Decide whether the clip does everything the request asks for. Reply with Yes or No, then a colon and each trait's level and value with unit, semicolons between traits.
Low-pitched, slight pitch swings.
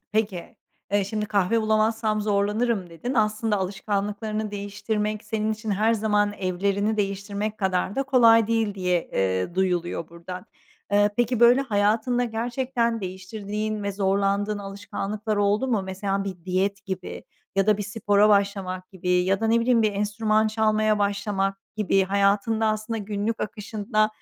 No: high, 205 Hz; narrow, 1.8 semitones